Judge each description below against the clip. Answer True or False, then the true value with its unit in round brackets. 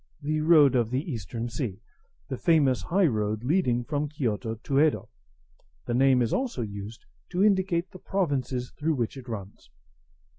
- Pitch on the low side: True (130 Hz)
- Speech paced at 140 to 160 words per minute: True (155 wpm)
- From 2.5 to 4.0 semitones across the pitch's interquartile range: False (5.3 semitones)